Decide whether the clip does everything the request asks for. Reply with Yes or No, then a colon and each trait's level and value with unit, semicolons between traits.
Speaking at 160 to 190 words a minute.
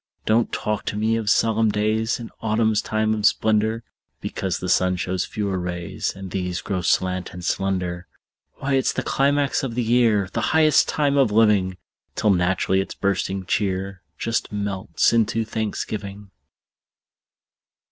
No: average, 150 wpm